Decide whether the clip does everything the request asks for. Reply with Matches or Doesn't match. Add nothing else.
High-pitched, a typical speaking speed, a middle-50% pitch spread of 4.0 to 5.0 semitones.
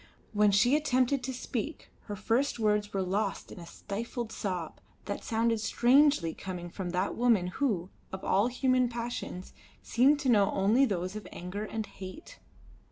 Matches